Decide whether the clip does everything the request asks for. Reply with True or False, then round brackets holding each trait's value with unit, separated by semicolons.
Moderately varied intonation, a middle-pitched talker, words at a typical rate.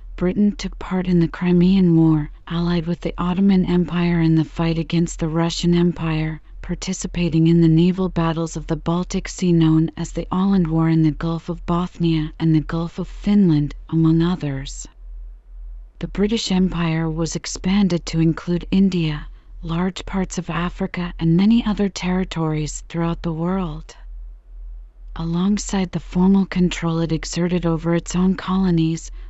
False (2.0 semitones; 170 Hz; 150 wpm)